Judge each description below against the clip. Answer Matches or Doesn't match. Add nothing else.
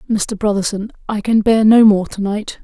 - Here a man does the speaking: Doesn't match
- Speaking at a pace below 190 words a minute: Doesn't match